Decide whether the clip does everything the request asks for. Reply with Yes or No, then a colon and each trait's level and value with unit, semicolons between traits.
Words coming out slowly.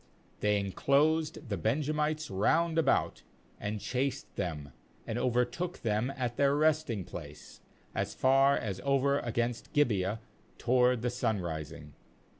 Yes: slow, 120 wpm